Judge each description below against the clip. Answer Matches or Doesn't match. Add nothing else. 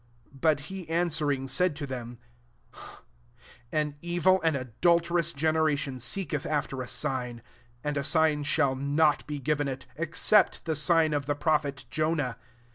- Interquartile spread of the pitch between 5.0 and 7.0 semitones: Doesn't match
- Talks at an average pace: Matches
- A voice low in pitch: Doesn't match